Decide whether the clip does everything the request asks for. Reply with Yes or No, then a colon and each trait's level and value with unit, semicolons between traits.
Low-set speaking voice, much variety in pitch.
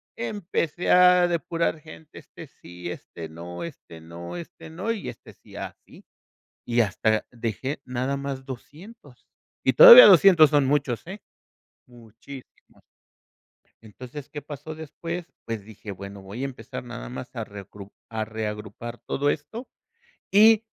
Yes: low, 130 Hz; wide, 7.5 semitones